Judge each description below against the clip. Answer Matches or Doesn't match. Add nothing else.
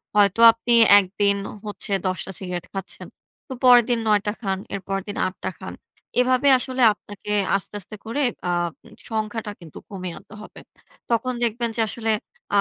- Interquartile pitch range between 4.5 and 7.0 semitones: Doesn't match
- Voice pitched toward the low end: Doesn't match